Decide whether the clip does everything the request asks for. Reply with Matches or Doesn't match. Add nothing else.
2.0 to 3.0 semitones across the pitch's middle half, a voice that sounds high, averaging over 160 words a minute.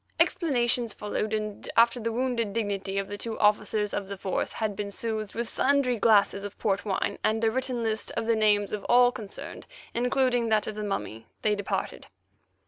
Matches